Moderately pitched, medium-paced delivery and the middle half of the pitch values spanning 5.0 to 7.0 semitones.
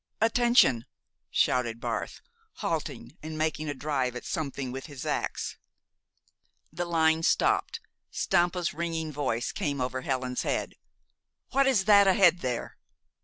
No: medium, 155 Hz; slow, 125 wpm; average, 5.3 semitones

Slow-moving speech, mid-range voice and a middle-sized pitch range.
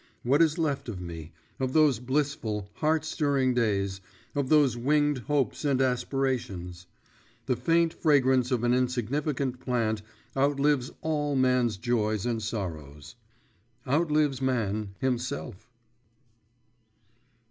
No: slow, 115 wpm; low, 125 Hz; average, 4.8 semitones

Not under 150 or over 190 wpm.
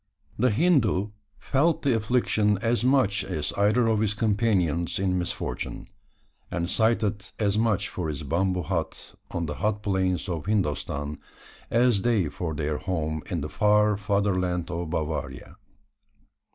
No: average, 140 wpm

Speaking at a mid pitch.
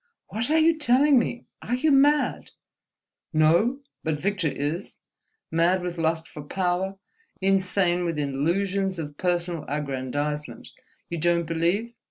Yes: medium, 175 Hz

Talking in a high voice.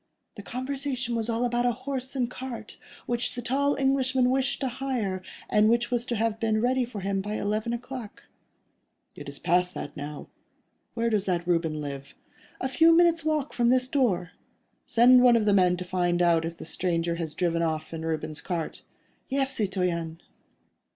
Yes: high, 225 Hz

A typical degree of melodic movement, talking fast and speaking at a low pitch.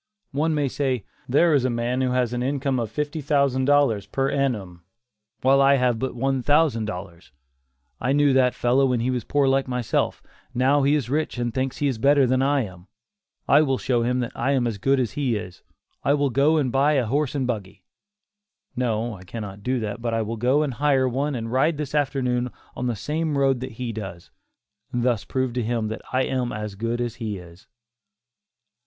Yes: average, 3.1 semitones; fast, 215 wpm; low, 125 Hz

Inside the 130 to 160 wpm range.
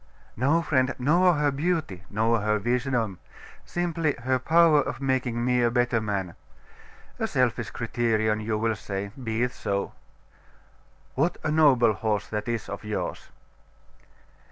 Yes: average, 140 wpm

